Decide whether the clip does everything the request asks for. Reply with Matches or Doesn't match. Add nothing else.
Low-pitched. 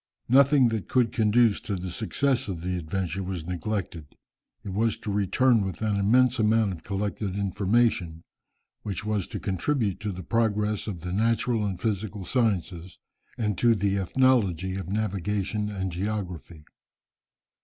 Matches